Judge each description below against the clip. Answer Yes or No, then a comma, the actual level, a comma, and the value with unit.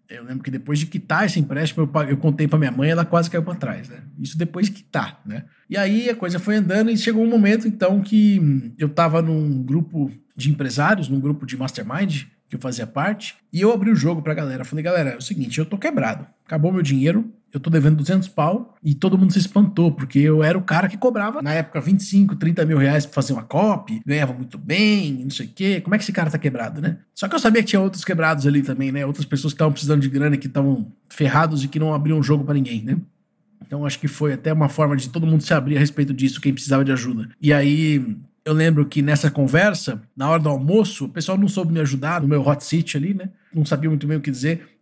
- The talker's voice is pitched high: No, medium, 155 Hz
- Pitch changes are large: No, average, 4.8 semitones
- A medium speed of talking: No, fast, 255 wpm